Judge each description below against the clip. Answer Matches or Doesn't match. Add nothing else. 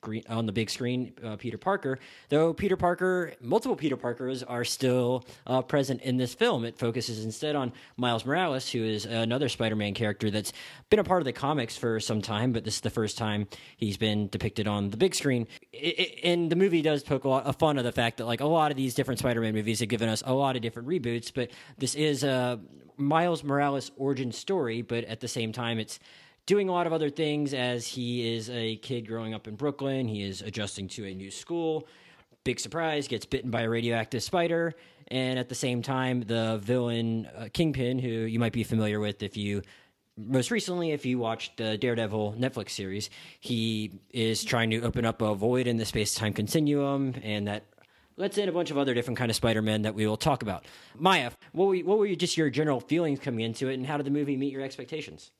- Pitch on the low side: Matches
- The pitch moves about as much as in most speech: Matches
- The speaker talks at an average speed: Doesn't match